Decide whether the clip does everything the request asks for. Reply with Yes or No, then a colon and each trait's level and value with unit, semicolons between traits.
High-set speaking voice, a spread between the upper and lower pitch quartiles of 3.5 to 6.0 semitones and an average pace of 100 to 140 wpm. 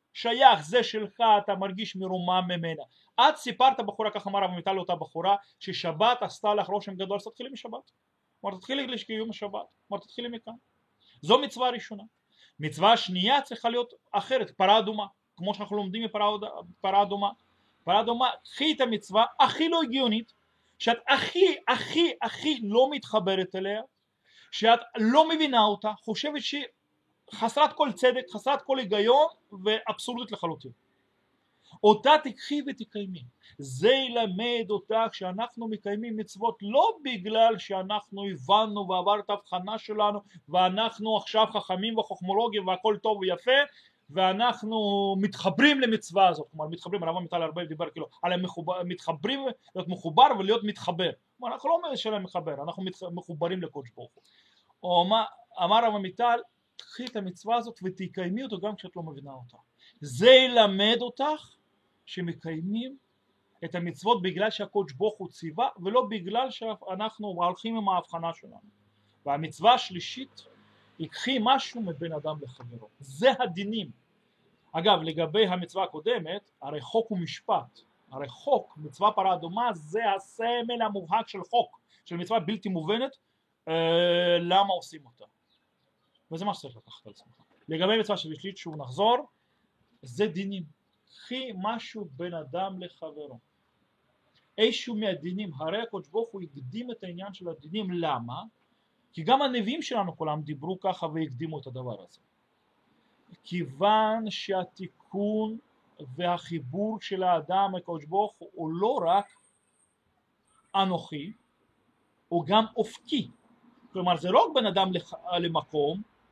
Yes: high, 205 Hz; average, 4.5 semitones; average, 130 wpm